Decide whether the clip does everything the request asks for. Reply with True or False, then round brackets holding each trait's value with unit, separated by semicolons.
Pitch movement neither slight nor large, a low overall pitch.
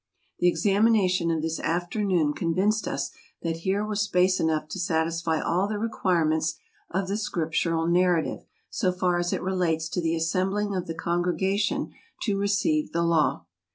False (3.1 semitones; 180 Hz)